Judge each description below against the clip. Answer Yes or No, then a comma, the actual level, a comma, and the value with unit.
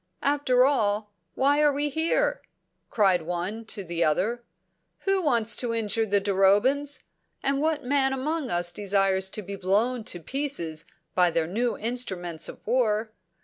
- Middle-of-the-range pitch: No, high, 225 Hz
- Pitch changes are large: Yes, wide, 6.2 semitones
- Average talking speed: Yes, average, 150 wpm